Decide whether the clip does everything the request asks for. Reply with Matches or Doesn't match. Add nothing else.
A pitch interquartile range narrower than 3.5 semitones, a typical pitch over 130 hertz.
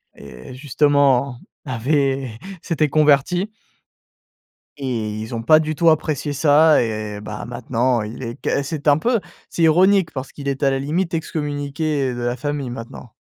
Doesn't match